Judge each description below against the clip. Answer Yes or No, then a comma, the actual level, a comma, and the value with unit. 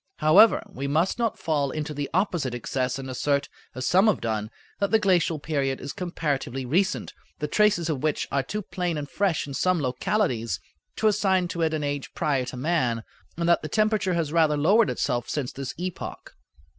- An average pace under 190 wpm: No, average, 195 wpm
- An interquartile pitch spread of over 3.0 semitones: Yes, average, 5.2 semitones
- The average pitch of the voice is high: No, medium, 155 Hz